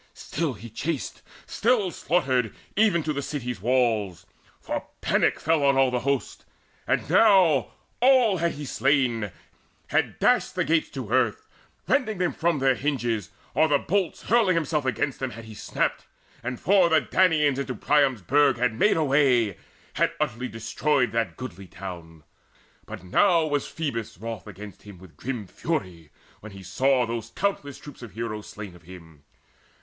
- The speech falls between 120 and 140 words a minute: No, average, 165 wpm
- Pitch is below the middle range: Yes, low, 130 Hz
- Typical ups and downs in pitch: No, wide, 6.1 semitones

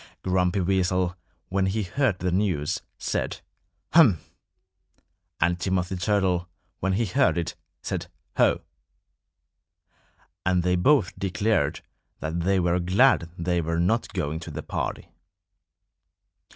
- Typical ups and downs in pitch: No, narrow, 2.1 semitones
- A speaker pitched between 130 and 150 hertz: No, very low, 90 Hz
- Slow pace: Yes, slow, 120 wpm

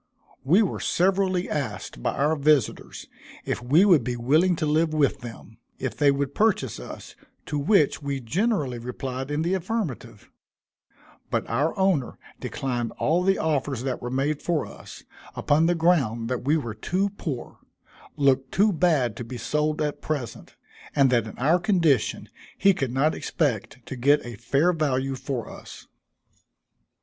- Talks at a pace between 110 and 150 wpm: No, average, 160 wpm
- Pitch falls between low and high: Yes, medium, 145 Hz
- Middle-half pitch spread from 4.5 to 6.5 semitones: Yes, average, 4.8 semitones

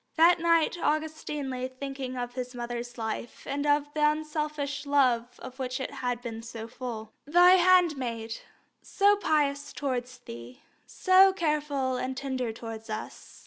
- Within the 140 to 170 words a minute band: Yes, average, 145 wpm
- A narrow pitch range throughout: No, average, 3.8 semitones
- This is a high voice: Yes, very high, 265 Hz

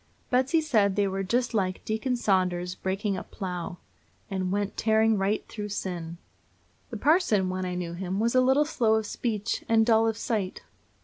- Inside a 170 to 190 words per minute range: Yes, average, 180 wpm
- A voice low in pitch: No, high, 205 Hz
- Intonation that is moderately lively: Yes, average, 3.4 semitones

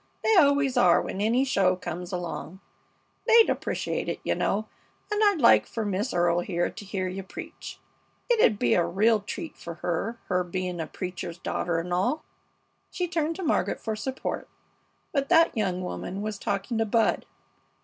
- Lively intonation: Yes, wide, 6.8 semitones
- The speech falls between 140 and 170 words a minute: No, average, 180 wpm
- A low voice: No, high, 205 Hz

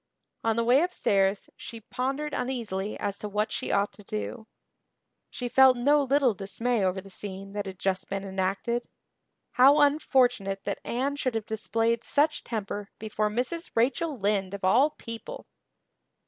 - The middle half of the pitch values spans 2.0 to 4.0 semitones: No, average, 4.5 semitones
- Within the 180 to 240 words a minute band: No, average, 160 wpm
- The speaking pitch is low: No, high, 225 Hz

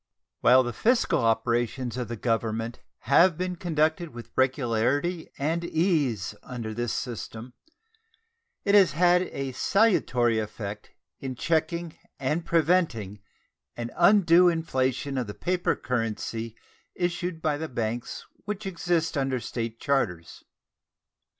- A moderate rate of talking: No, slow, 120 wpm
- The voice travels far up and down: Yes, wide, 6.4 semitones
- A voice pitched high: No, low, 135 Hz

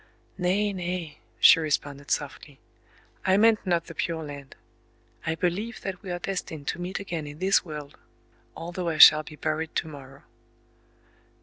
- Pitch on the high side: No, medium, 165 Hz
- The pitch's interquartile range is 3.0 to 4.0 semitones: Yes, average, 3.5 semitones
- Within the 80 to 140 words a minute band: No, average, 150 wpm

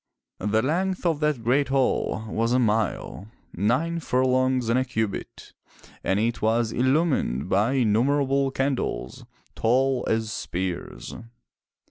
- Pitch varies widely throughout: No, average, 3.6 semitones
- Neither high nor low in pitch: No, low, 125 Hz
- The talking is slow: Yes, slow, 125 wpm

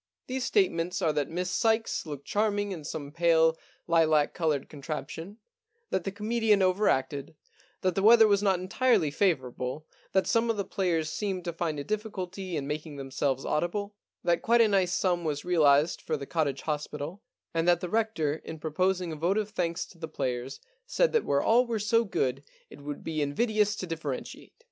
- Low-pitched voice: No, medium, 175 Hz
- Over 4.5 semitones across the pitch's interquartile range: Yes, average, 5.3 semitones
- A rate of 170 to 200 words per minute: Yes, average, 185 wpm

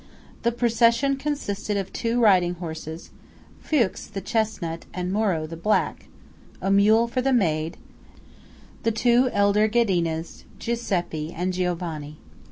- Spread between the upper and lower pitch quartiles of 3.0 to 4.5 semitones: No, average, 5.2 semitones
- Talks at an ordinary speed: No, slow, 125 wpm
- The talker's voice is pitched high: Yes, high, 200 Hz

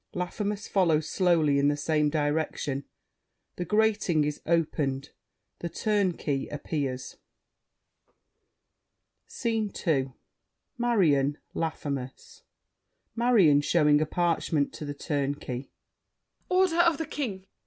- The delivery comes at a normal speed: No, slow, 100 wpm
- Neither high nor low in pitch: Yes, medium, 160 Hz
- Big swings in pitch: Yes, wide, 6.0 semitones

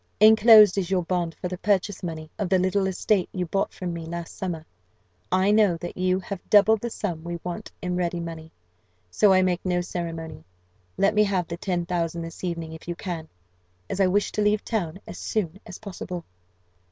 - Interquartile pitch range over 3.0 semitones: No, average, 2.7 semitones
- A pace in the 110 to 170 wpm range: No, average, 200 wpm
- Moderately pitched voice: Yes, medium, 180 Hz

